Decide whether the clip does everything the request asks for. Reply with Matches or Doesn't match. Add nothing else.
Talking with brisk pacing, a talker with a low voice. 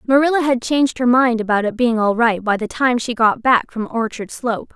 Doesn't match